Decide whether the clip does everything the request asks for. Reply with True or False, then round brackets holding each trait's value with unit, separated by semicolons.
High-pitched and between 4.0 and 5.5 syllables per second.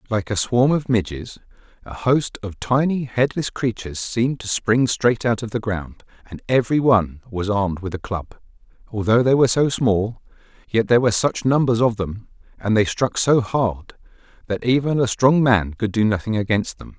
False (115 Hz; 5.1 syllables/s)